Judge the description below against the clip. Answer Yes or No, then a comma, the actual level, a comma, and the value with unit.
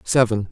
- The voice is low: Yes, low, 115 Hz